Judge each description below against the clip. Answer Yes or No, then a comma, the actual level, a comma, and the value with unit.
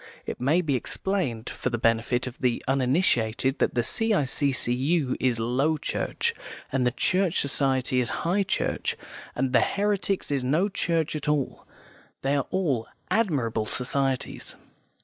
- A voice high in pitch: No, low, 135 Hz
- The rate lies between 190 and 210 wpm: No, average, 145 wpm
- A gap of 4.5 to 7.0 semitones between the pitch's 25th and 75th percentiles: Yes, average, 4.9 semitones